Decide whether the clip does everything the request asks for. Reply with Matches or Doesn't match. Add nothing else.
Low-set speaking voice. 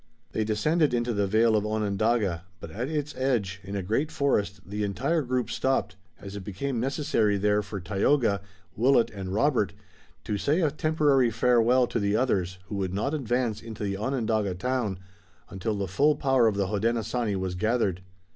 Matches